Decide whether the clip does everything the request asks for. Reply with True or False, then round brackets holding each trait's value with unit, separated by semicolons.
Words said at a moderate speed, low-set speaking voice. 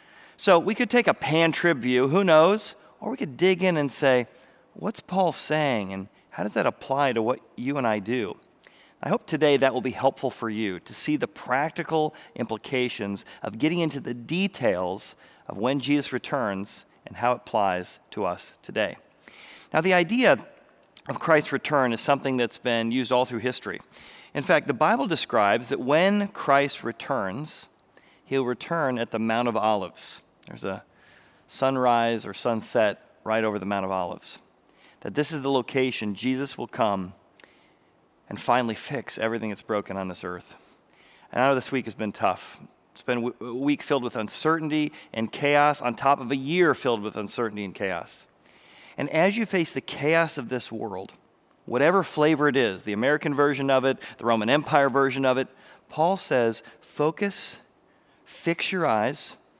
True (175 wpm; 130 Hz)